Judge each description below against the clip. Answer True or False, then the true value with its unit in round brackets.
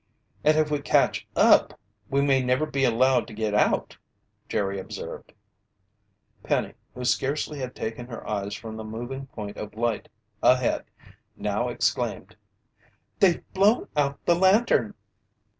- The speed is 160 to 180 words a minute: False (140 wpm)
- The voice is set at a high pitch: False (125 Hz)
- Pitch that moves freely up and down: False (4.5 semitones)